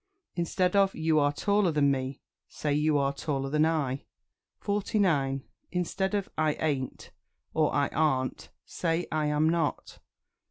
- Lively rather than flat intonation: No, average, 3.5 semitones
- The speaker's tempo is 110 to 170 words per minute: Yes, average, 145 wpm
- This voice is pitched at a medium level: Yes, medium, 155 Hz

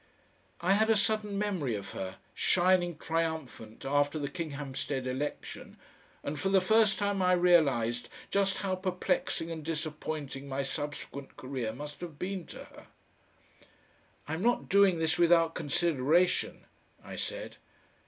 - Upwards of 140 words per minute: No, slow, 135 wpm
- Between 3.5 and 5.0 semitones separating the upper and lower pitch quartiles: Yes, average, 4.6 semitones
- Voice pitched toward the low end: No, medium, 165 Hz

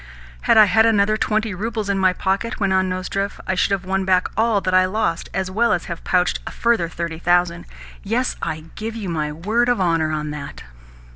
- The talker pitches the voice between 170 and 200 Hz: Yes, high, 190 Hz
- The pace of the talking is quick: Yes, fast, 220 wpm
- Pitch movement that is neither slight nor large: Yes, average, 3.7 semitones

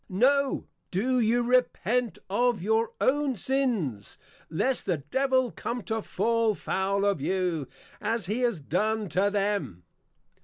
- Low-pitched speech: No, high, 220 Hz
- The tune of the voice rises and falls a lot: No, average, 4.6 semitones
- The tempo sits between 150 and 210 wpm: No, average, 140 wpm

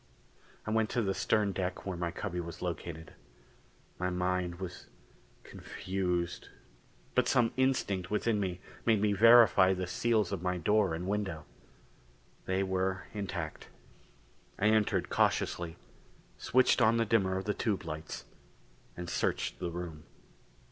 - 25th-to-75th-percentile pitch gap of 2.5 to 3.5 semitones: Yes, average, 3.2 semitones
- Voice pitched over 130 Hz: No, very low, 95 Hz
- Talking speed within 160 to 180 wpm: No, average, 140 wpm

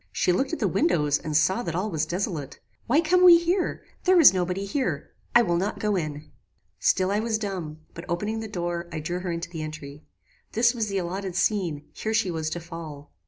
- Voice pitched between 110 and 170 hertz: No, medium, 180 Hz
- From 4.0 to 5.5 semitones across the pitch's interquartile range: Yes, average, 5.2 semitones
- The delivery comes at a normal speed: No, fast, 220 wpm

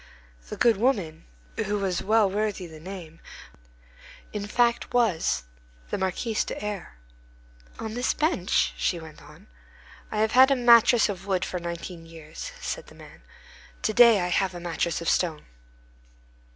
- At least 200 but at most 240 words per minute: No, average, 155 wpm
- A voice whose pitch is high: Yes, high, 195 Hz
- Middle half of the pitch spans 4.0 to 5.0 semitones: Yes, average, 4.6 semitones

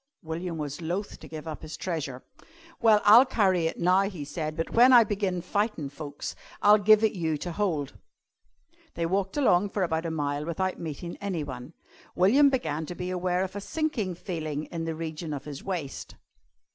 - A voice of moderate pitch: Yes, medium, 175 Hz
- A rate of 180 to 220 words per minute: Yes, average, 185 wpm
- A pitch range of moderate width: Yes, average, 4.2 semitones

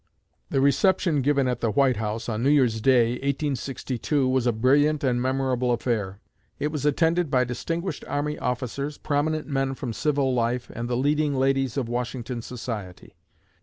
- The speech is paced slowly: No, average, 165 wpm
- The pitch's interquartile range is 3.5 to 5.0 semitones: No, average, 3.1 semitones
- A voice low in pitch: Yes, low, 130 Hz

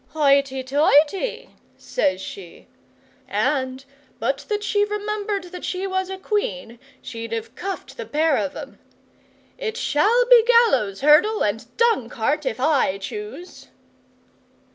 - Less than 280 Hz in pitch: No, very high, 300 Hz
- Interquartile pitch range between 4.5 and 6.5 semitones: No, wide, 8.5 semitones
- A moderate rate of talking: No, slow, 125 wpm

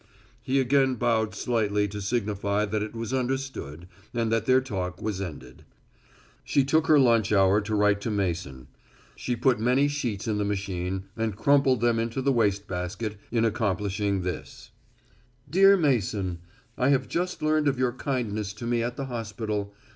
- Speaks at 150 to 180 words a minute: Yes, average, 170 wpm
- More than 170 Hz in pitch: No, low, 110 Hz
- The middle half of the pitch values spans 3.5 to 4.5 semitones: Yes, average, 4.2 semitones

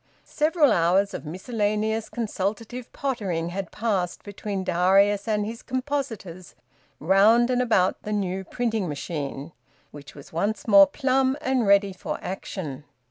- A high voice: Yes, high, 205 Hz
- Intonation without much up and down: No, average, 4.3 semitones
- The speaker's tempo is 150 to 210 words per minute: No, slow, 135 wpm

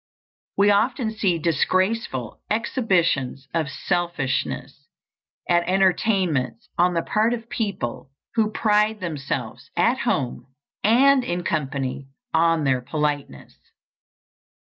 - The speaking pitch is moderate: Yes, medium, 175 Hz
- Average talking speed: No, slow, 100 wpm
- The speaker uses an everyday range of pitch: No, wide, 7.4 semitones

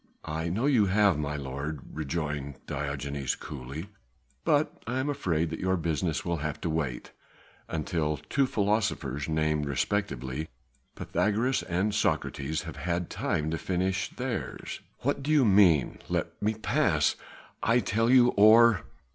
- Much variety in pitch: Yes, wide, 6.1 semitones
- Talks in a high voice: No, very low, 85 Hz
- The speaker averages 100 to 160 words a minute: Yes, average, 140 wpm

